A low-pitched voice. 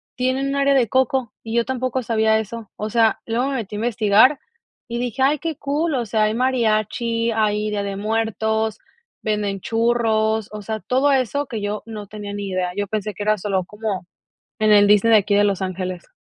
No: high, 220 Hz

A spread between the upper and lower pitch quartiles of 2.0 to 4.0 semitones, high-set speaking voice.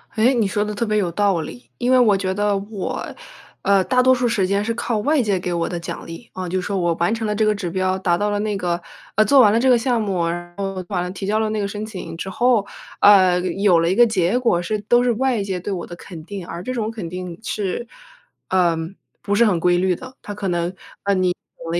Yes: average, 3.4 semitones; high, 200 Hz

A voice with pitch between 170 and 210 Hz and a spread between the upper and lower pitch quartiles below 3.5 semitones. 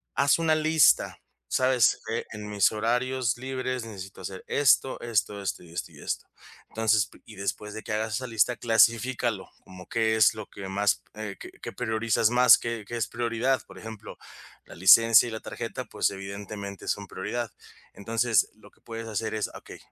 No: low, 110 Hz; average, 2.9 semitones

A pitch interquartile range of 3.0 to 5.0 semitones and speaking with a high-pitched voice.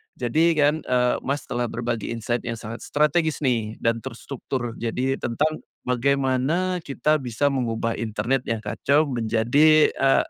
No: average, 3.7 semitones; low, 125 Hz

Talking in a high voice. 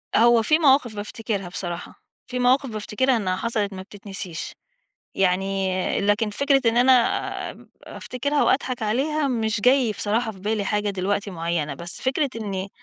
Yes: high, 215 Hz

